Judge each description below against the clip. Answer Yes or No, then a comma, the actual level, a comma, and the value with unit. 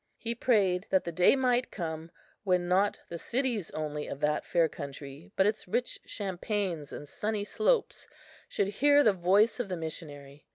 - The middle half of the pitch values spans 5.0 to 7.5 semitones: Yes, average, 5.3 semitones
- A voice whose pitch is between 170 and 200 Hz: Yes, medium, 185 Hz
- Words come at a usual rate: Yes, average, 170 wpm